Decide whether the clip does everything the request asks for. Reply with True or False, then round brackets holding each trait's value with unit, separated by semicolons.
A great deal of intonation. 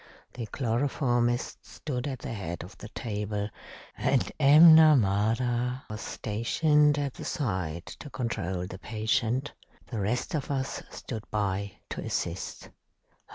False (4.7 semitones)